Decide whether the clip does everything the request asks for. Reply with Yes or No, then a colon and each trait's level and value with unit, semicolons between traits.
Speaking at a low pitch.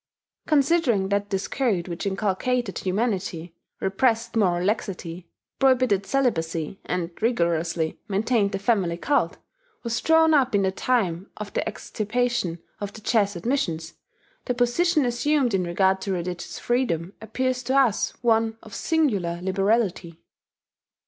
No: high, 205 Hz